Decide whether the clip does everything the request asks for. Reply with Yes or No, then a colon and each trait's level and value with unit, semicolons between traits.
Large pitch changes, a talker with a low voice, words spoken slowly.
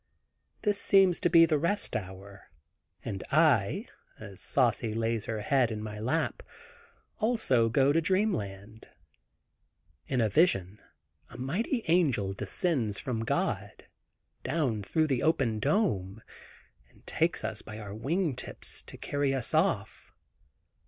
Yes: wide, 7.5 semitones; low, 125 Hz; slow, 130 wpm